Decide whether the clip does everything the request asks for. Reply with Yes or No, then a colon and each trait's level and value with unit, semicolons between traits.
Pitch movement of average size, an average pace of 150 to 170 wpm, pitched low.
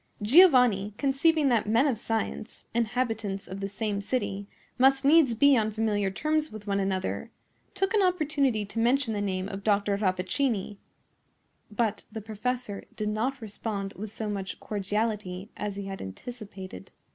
No: average, 4.0 semitones; average, 155 wpm; high, 215 Hz